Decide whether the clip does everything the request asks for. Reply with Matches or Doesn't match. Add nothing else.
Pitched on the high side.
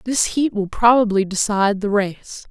Matches